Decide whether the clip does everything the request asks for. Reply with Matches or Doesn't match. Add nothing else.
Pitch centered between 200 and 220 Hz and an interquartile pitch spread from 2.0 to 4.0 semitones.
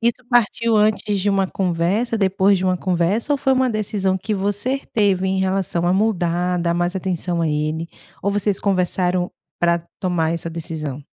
Doesn't match